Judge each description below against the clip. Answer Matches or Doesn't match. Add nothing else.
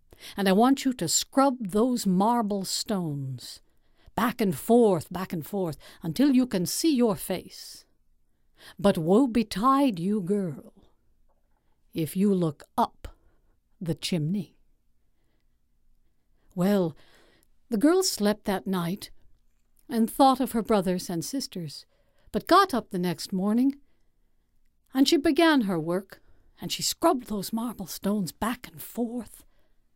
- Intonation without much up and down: Doesn't match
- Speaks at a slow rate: Matches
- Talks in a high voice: Matches